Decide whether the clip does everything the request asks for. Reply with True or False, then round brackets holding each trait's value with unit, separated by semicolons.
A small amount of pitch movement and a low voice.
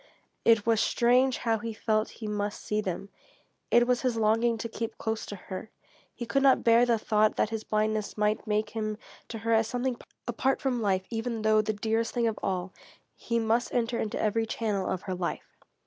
False (1.7 semitones; 225 Hz)